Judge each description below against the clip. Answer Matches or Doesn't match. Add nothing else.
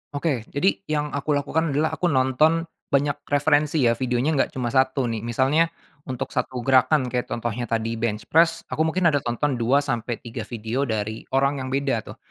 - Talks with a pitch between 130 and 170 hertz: Matches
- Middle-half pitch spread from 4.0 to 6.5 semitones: Doesn't match